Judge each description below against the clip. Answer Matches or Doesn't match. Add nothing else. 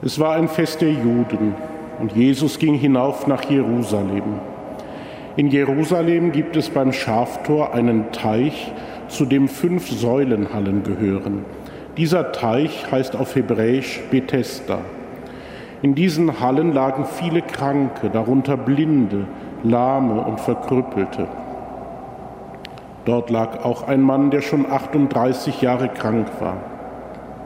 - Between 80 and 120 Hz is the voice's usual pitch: Doesn't match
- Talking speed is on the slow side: Matches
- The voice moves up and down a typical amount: Matches